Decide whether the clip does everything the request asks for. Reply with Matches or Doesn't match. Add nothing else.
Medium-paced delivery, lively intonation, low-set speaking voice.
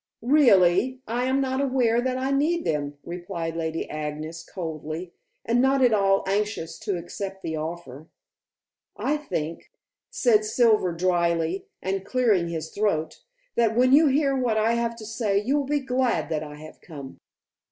Doesn't match